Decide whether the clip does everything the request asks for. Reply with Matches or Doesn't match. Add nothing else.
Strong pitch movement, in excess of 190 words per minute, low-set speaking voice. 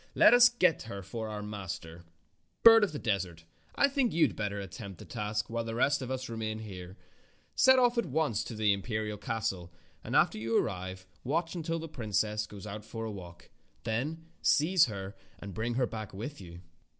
Matches